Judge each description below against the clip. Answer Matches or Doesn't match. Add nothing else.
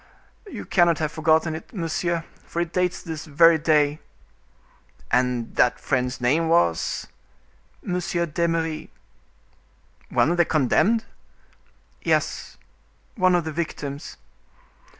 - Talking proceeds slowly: Matches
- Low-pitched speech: Doesn't match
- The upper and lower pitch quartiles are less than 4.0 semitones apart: Matches